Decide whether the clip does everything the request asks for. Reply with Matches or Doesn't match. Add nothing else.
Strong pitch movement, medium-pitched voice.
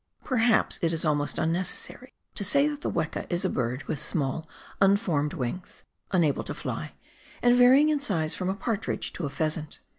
Matches